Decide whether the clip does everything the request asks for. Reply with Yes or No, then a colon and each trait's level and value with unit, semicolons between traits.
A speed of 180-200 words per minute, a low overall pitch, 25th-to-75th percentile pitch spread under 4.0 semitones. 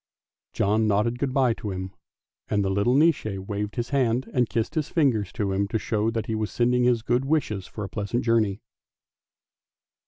Yes: average, 190 wpm; low, 110 Hz; average, 3.3 semitones